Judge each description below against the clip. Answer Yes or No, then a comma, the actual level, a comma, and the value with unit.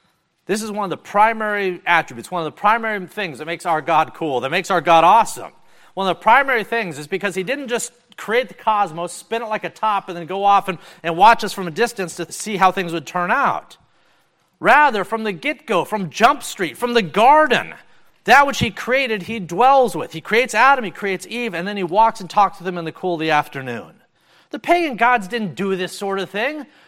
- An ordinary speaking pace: No, fast, 235 wpm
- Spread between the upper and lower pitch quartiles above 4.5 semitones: Yes, average, 4.9 semitones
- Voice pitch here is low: No, high, 200 Hz